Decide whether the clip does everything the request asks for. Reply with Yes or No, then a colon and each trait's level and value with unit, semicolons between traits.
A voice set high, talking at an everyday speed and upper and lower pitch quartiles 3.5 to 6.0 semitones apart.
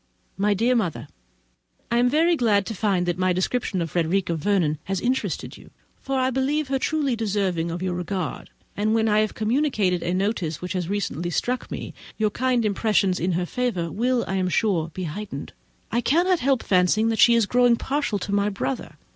Yes: high, 205 Hz; average, 195 wpm; average, 5.2 semitones